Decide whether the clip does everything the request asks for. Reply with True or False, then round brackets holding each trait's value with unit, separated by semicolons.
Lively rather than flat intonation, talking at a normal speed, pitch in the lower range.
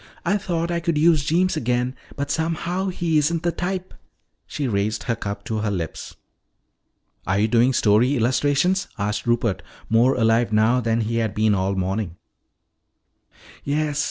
True (6.8 semitones; 155 wpm; 125 Hz)